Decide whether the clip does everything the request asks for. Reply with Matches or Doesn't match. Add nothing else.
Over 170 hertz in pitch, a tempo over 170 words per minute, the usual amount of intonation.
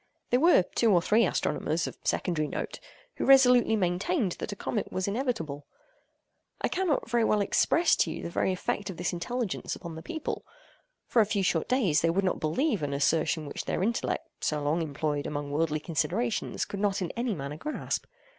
Doesn't match